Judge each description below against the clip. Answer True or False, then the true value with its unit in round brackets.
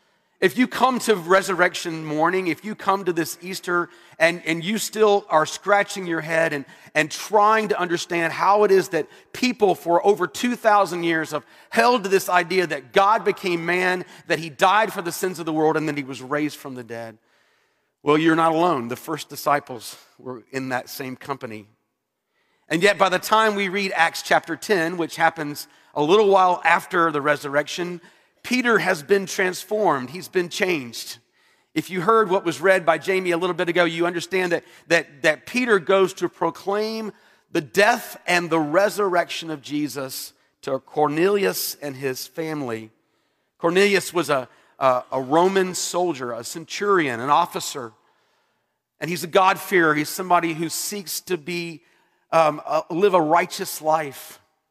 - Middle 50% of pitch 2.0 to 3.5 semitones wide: False (3.9 semitones)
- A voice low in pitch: False (170 Hz)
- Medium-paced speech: True (170 wpm)